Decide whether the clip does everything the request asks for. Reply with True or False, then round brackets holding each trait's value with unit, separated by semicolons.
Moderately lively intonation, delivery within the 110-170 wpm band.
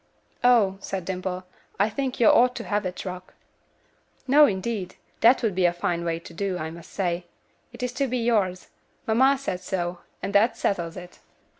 False (4.7 semitones; 185 wpm)